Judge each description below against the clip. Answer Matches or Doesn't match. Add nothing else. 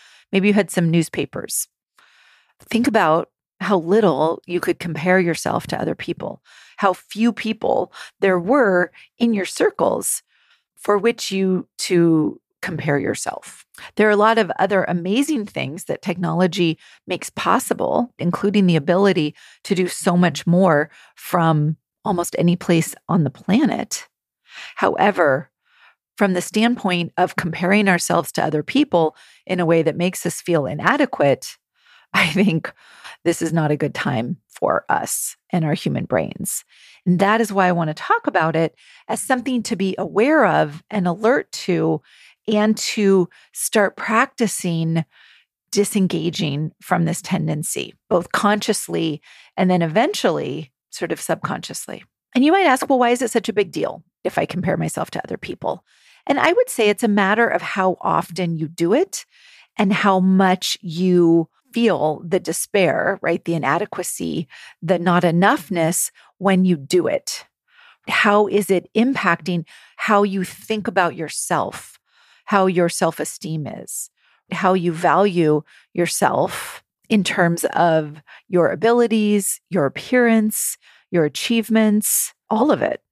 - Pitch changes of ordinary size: Matches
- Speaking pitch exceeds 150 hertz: Matches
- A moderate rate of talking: Matches